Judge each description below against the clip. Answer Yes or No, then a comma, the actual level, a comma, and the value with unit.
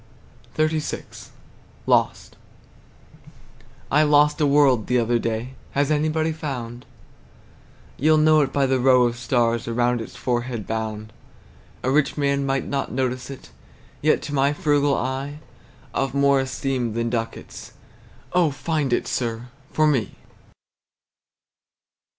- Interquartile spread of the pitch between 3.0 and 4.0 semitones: Yes, average, 3.4 semitones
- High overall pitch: No, low, 135 Hz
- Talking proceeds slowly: Yes, slow, 125 wpm